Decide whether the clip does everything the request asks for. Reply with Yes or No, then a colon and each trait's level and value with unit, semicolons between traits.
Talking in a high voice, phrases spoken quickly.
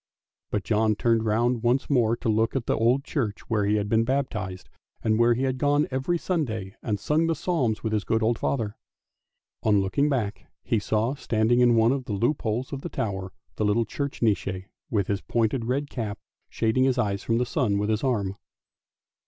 No: low, 115 Hz; fast, 210 wpm